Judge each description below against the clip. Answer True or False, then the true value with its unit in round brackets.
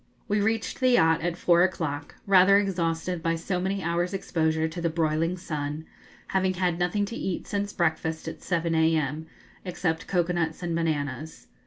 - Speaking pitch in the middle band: True (170 Hz)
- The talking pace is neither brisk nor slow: True (170 wpm)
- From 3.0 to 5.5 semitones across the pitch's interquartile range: False (2.5 semitones)